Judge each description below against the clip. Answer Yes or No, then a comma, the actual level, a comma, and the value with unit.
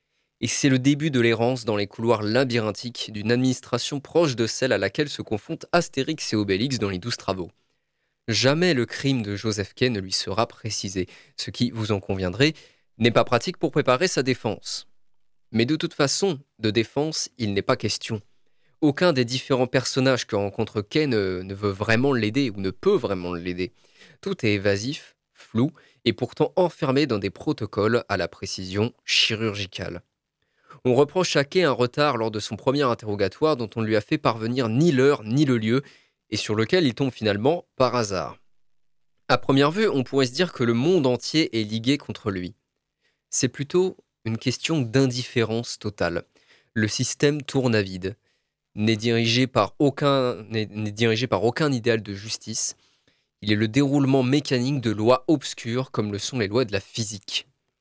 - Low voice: Yes, low, 120 Hz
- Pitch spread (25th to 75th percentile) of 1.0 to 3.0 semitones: No, average, 4.4 semitones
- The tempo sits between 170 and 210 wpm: Yes, average, 180 wpm